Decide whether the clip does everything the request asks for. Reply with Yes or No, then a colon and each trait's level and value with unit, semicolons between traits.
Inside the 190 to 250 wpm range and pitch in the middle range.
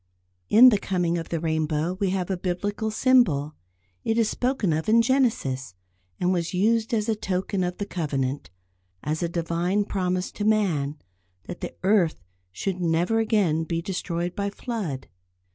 No: average, 160 wpm; medium, 180 Hz